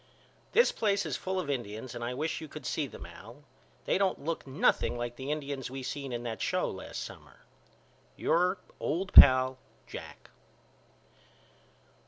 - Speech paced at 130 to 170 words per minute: Yes, average, 160 wpm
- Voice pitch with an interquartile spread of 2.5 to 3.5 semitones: No, average, 5.0 semitones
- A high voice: No, low, 135 Hz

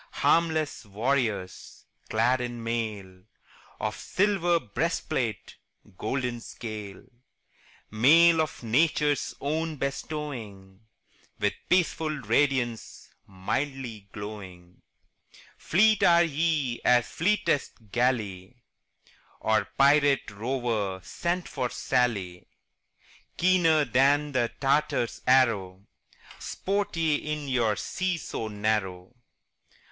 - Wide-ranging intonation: Yes, wide, 6.0 semitones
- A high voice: No, low, 125 Hz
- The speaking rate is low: Yes, slow, 90 wpm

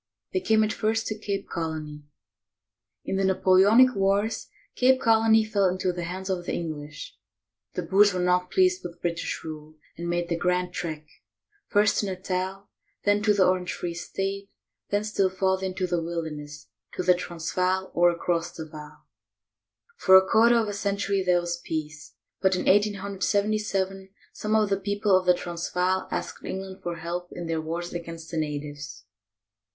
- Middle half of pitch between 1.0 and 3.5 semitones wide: Yes, average, 2.9 semitones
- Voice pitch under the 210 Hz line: Yes, medium, 185 Hz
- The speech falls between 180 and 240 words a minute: No, average, 170 wpm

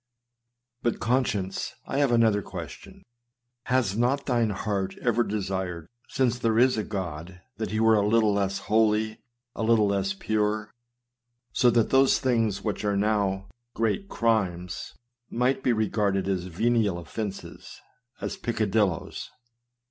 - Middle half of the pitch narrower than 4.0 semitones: Yes, average, 3.0 semitones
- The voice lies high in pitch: No, low, 110 Hz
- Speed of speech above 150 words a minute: No, slow, 135 wpm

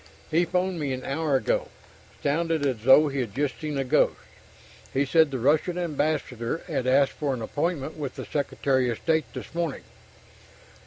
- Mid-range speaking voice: Yes, medium, 145 Hz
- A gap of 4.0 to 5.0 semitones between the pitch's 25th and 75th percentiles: No, average, 3.3 semitones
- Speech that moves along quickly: No, average, 170 wpm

